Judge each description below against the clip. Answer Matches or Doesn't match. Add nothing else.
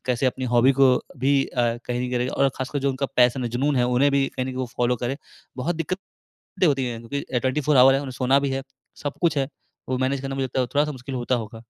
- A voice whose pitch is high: Doesn't match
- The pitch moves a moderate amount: Doesn't match